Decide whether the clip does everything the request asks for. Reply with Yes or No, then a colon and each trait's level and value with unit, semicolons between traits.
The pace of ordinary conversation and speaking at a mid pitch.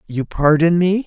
Yes: average, 170 wpm; medium, 165 Hz